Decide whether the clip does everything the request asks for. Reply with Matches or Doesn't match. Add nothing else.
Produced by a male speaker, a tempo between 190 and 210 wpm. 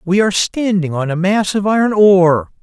Matches